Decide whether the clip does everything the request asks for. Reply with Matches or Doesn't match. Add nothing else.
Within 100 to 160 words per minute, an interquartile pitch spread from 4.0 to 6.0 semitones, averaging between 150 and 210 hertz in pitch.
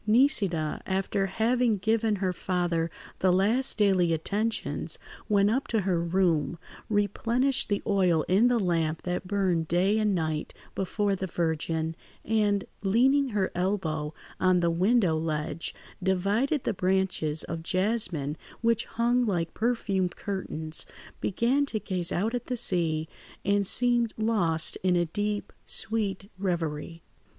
Matches